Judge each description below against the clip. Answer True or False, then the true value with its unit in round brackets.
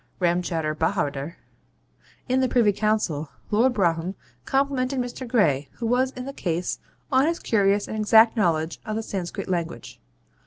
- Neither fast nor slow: True (150 wpm)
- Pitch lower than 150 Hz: False (205 Hz)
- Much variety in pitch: True (6.6 semitones)